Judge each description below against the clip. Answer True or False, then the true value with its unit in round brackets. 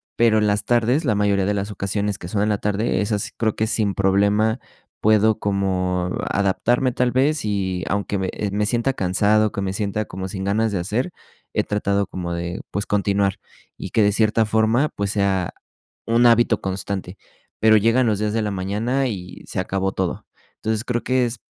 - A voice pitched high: False (105 Hz)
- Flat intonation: True (2.3 semitones)